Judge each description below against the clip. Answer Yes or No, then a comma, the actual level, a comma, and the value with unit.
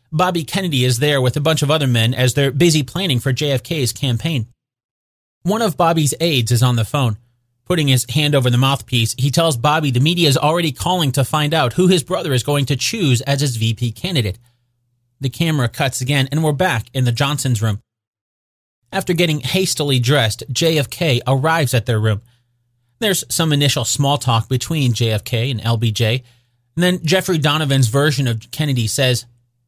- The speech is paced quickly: No, average, 180 wpm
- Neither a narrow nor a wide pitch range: Yes, average, 4.4 semitones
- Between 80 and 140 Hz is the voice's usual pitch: Yes, low, 135 Hz